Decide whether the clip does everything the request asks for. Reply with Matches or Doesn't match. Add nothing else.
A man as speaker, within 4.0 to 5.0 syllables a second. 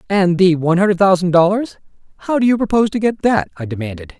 Doesn't match